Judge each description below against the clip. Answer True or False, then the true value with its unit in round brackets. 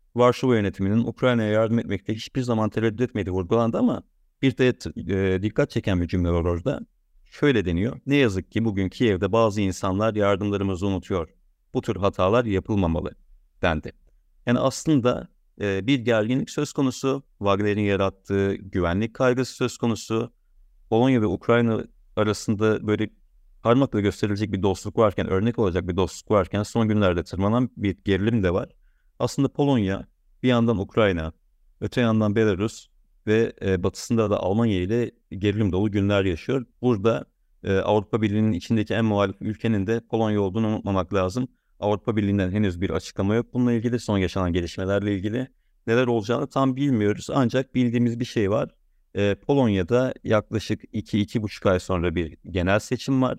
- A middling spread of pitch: True (3.4 semitones)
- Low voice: True (105 Hz)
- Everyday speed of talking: False (145 wpm)